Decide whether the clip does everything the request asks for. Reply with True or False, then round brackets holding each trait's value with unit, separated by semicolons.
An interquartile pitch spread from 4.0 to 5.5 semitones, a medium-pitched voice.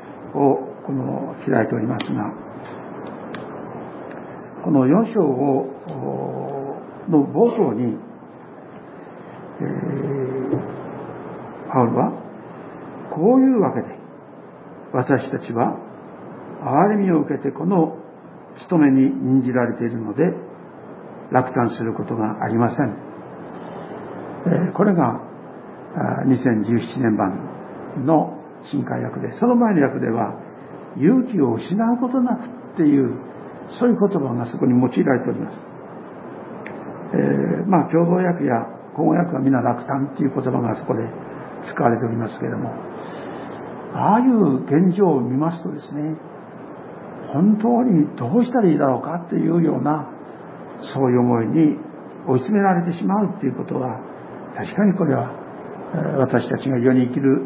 False (7.0 semitones; 145 Hz)